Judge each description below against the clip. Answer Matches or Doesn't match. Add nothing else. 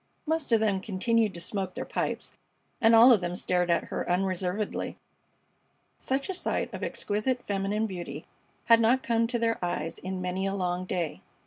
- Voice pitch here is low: Doesn't match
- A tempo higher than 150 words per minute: Matches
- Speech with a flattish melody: Doesn't match